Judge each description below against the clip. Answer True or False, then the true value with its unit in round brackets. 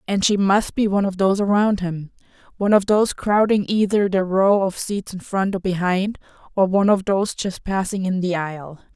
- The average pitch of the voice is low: False (195 Hz)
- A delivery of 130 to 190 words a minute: False (200 wpm)